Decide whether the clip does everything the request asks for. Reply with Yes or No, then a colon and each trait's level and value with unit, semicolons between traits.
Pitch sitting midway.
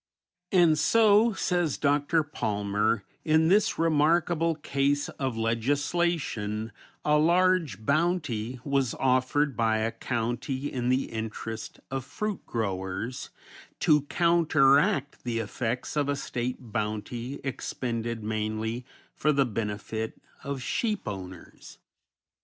No: low, 130 Hz